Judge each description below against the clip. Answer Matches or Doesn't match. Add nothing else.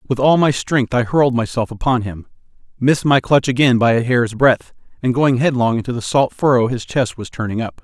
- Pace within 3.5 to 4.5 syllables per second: Doesn't match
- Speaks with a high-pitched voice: Doesn't match